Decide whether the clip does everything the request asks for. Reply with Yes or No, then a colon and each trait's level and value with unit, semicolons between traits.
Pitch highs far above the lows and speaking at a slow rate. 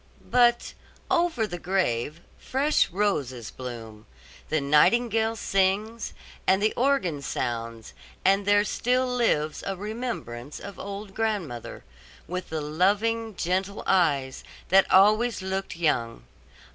Yes: wide, 6.9 semitones; slow, 115 wpm